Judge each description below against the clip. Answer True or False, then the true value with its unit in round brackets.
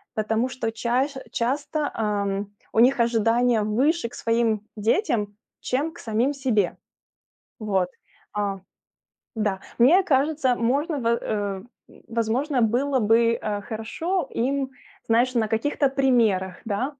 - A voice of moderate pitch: False (235 Hz)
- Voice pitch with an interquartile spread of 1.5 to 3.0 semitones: False (3.8 semitones)